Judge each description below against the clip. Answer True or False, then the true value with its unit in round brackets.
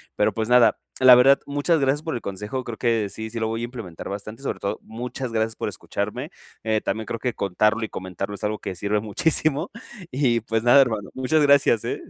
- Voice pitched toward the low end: True (115 Hz)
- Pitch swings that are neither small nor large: True (3.4 semitones)